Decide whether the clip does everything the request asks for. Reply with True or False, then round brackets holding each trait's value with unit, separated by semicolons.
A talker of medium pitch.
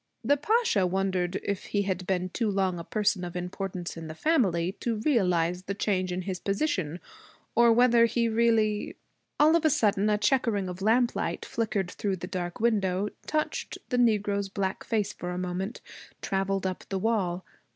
False (195 Hz)